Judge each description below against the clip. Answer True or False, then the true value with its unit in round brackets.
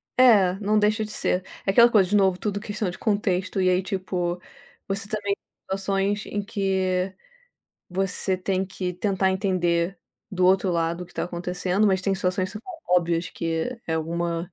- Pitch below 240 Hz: True (190 Hz)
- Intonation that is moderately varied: False (2.1 semitones)